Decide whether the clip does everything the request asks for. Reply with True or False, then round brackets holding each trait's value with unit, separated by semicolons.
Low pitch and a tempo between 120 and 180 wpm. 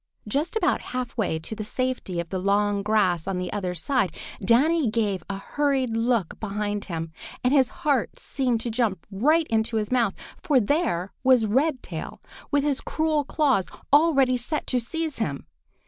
False (235 Hz; 170 wpm)